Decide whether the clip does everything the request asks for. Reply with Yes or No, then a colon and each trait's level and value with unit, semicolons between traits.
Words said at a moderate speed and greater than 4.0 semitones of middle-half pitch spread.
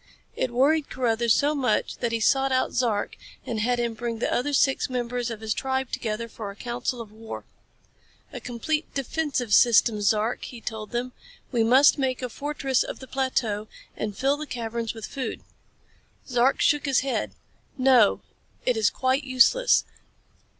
No: average, 170 wpm; average, 2.8 semitones